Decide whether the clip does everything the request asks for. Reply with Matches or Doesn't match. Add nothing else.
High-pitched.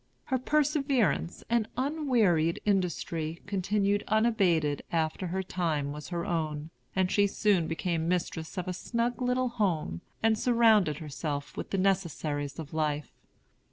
Doesn't match